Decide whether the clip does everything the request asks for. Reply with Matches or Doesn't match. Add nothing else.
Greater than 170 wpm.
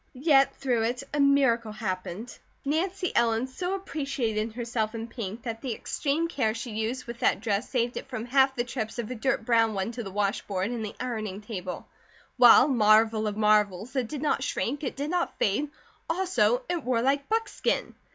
Matches